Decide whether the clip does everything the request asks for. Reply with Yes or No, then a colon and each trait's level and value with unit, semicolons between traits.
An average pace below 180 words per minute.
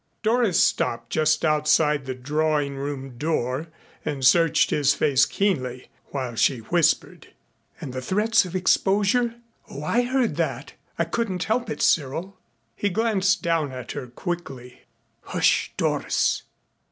Yes: average, 140 wpm